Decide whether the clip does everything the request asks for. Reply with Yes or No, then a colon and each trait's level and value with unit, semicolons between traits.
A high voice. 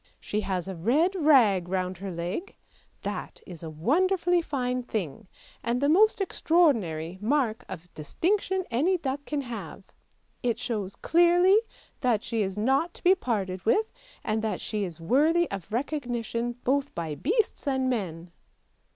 Yes: high, 240 Hz